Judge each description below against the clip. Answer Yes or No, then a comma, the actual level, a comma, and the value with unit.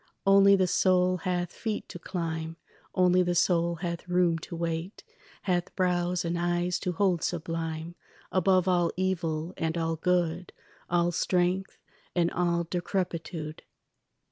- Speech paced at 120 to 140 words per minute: Yes, slow, 135 wpm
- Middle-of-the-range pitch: Yes, medium, 175 Hz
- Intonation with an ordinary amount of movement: No, narrow, 1.4 semitones